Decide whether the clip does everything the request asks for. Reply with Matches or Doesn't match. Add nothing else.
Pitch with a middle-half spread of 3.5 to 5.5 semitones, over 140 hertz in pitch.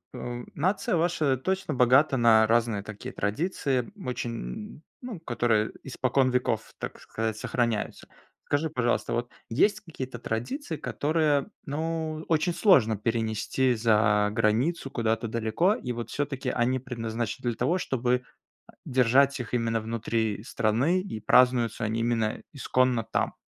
Doesn't match